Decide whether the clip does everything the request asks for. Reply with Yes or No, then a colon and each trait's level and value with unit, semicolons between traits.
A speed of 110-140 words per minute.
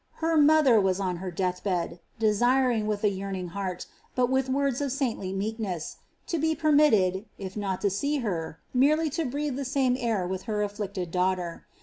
No: average, 185 wpm